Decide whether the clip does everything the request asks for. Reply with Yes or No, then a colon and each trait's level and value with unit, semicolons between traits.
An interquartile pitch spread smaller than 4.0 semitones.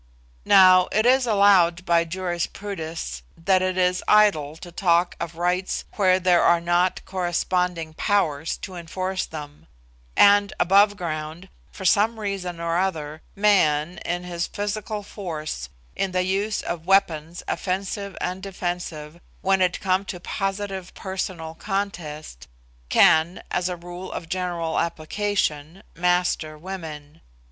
Yes: average, 2.7 semitones